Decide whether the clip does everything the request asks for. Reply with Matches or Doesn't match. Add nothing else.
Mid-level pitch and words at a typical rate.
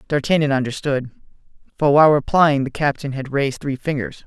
Matches